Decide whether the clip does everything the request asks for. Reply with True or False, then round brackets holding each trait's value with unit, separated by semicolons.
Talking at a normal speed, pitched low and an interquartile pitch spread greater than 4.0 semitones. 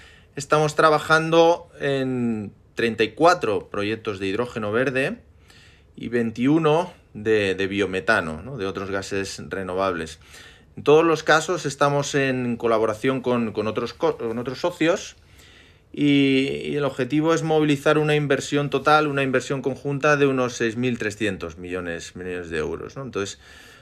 True (135 wpm; 130 Hz; 5.6 semitones)